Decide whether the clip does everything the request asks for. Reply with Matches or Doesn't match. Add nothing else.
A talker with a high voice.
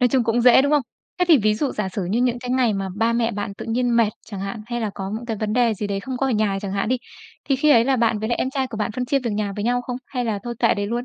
Matches